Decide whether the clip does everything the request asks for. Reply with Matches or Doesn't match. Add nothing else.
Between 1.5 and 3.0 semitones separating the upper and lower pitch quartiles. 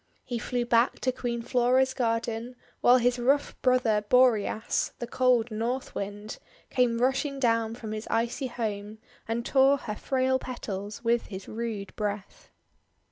Matches